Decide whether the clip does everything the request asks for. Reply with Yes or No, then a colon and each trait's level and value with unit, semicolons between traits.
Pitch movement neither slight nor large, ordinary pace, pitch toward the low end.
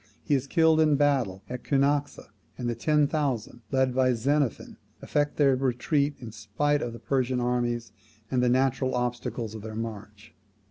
Yes: average, 3.3 semitones; average, 170 wpm; low, 130 Hz